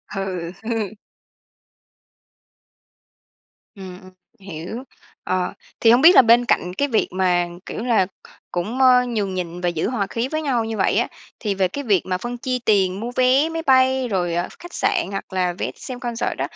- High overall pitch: Yes, high, 220 Hz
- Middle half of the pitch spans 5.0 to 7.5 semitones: Yes, average, 5.3 semitones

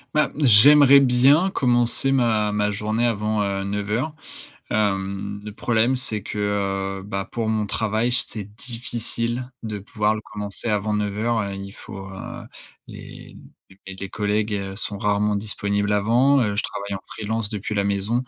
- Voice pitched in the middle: No, low, 105 Hz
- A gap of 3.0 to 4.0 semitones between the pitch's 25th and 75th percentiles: No, narrow, 2.6 semitones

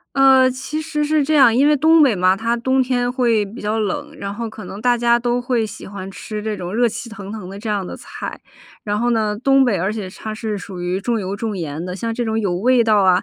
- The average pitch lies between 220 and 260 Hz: Yes, high, 225 Hz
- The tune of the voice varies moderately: Yes, average, 3.8 semitones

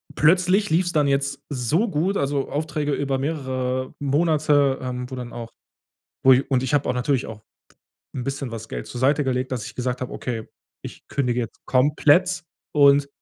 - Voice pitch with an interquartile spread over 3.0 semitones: No, average, 2.7 semitones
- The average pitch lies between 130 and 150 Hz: Yes, low, 135 Hz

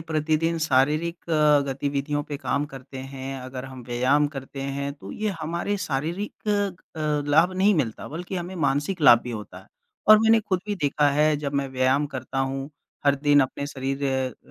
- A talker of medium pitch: Yes, medium, 145 Hz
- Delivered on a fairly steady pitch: No, average, 3.0 semitones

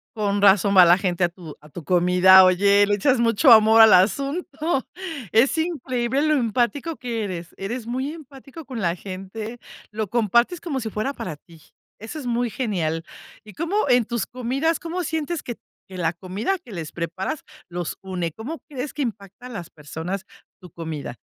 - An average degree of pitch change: No, wide, 6.3 semitones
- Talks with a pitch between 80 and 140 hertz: No, high, 220 Hz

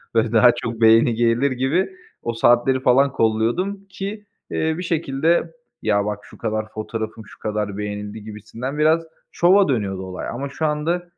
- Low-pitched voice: Yes, low, 120 Hz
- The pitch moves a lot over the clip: Yes, wide, 6.3 semitones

